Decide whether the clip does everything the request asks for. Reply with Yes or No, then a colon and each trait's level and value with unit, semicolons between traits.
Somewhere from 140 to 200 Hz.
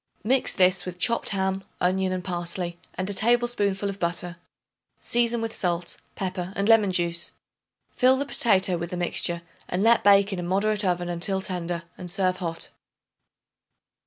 Yes: high, 190 Hz